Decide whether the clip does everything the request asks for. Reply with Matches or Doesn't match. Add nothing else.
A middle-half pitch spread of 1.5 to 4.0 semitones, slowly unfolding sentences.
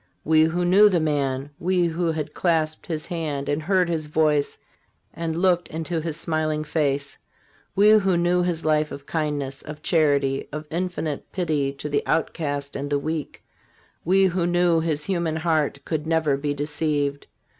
Doesn't match